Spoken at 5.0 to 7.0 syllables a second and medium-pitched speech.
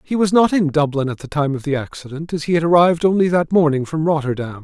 Yes: 6.4 syllables/s; medium, 155 Hz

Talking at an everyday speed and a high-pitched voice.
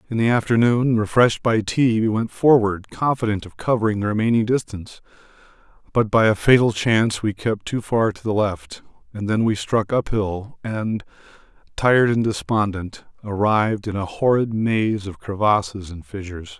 No: average, 165 wpm; low, 110 Hz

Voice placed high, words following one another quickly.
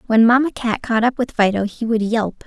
Yes: high, 230 Hz; fast, 245 wpm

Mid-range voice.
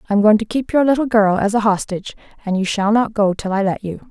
No: high, 210 Hz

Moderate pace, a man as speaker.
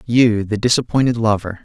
Yes: average, 145 wpm; male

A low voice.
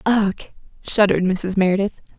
No: high, 195 Hz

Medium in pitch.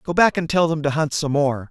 Yes: medium, 150 Hz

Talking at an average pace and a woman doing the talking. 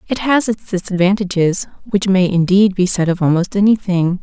Yes: average, 170 wpm; female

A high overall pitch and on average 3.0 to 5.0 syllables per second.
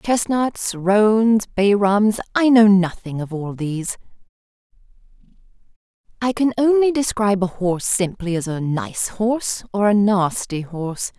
Yes: high, 200 Hz; 4.2 syllables/s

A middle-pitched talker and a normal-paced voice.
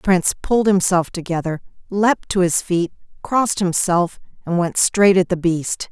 Yes: medium, 180 Hz; average, 170 wpm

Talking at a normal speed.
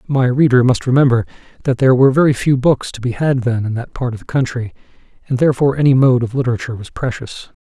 No: fast, 220 wpm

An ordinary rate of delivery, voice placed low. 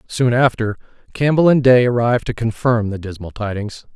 Yes: average, 165 wpm; low, 120 Hz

